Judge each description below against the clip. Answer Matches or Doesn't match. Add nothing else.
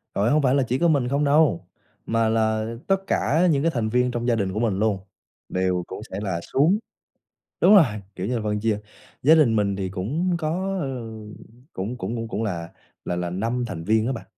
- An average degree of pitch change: Doesn't match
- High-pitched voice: Doesn't match